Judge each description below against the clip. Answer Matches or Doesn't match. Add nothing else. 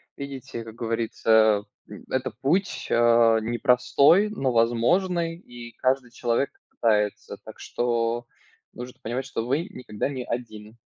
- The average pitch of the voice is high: Doesn't match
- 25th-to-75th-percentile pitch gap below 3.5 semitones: Matches